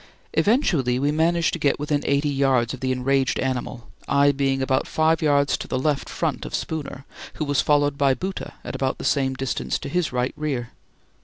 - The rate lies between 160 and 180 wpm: No, average, 200 wpm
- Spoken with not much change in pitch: Yes, narrow, 2.1 semitones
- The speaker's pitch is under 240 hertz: Yes, medium, 140 Hz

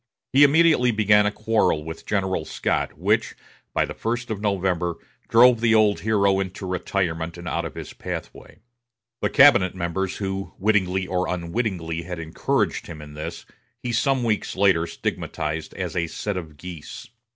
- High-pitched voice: No, very low, 95 Hz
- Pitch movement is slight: No, average, 4.3 semitones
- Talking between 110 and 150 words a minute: No, average, 165 wpm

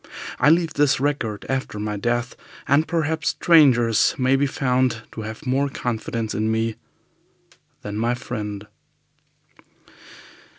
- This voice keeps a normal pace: No, slow, 125 wpm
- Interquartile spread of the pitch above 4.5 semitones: No, average, 4.2 semitones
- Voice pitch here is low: Yes, low, 125 Hz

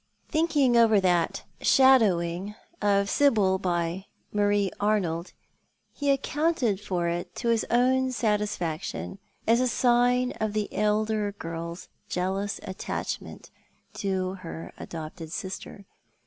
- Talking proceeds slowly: Yes, slow, 120 wpm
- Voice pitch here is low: No, high, 205 Hz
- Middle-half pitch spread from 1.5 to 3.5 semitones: No, average, 4.6 semitones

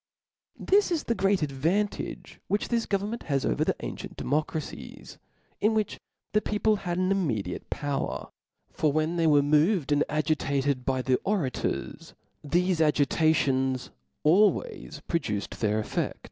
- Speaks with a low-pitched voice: No, medium, 155 Hz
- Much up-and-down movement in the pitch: Yes, wide, 6.1 semitones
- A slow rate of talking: No, average, 145 wpm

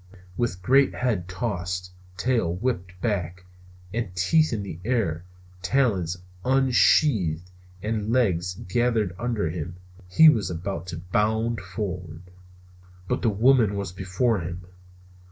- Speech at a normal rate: No, slow, 120 wpm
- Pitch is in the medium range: No, very low, 95 Hz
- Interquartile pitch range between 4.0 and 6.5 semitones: Yes, average, 4.7 semitones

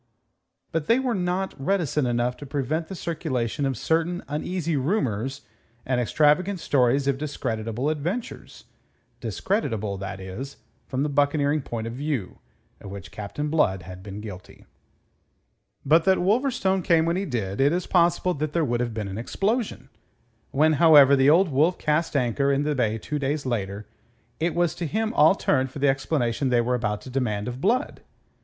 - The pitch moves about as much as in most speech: No, wide, 5.7 semitones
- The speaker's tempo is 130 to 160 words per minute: No, average, 175 wpm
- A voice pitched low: No, medium, 145 Hz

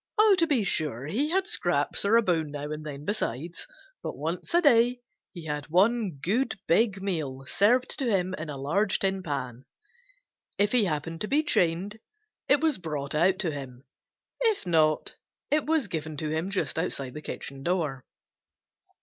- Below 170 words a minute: No, average, 175 wpm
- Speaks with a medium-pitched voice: Yes, medium, 175 Hz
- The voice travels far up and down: Yes, wide, 6.7 semitones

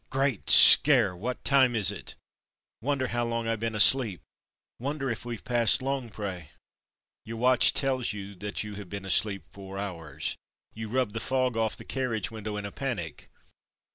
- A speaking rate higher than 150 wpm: Yes, average, 170 wpm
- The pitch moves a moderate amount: Yes, average, 4.0 semitones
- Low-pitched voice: Yes, low, 115 Hz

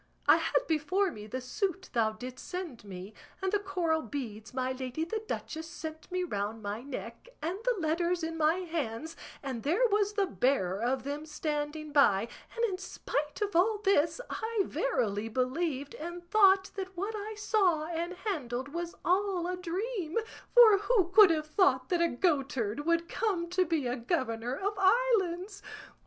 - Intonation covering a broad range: Yes, wide, 6.5 semitones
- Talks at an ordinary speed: Yes, average, 175 wpm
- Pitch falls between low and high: No, very high, 330 Hz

